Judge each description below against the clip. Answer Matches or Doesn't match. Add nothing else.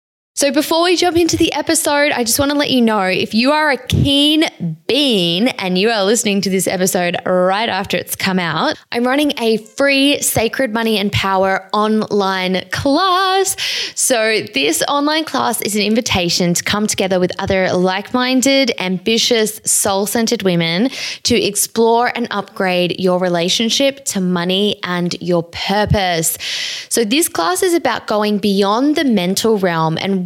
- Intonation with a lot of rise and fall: Matches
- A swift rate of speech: Doesn't match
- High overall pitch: Matches